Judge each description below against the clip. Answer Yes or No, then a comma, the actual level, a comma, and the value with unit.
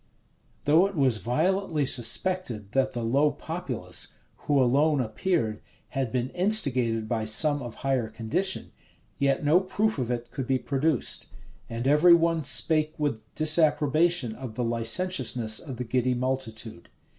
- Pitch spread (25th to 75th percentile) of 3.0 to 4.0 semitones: No, average, 5.1 semitones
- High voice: No, low, 135 Hz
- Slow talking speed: No, average, 145 wpm